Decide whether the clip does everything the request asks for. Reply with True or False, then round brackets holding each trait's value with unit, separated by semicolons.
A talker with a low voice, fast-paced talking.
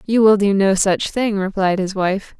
False (200 Hz; 225 wpm)